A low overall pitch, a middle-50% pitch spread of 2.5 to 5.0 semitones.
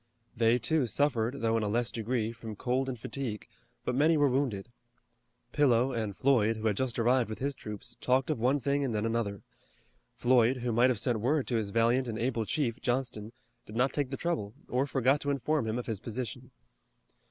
Yes: low, 120 Hz; average, 2.9 semitones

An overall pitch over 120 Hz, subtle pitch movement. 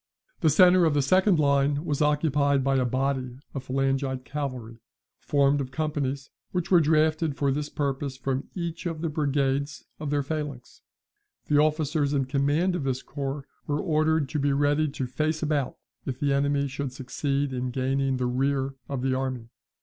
Yes: medium, 140 Hz; narrow, 2.2 semitones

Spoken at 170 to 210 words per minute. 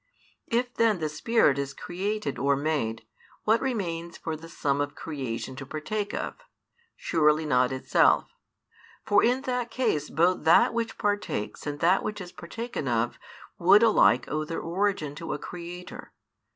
No: average, 155 wpm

